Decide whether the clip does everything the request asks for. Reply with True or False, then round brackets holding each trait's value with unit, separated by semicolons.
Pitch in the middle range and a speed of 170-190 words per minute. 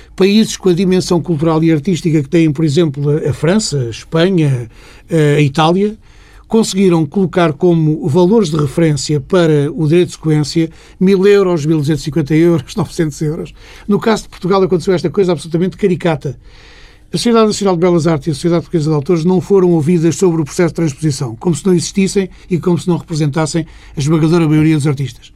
True (165 Hz; 185 wpm)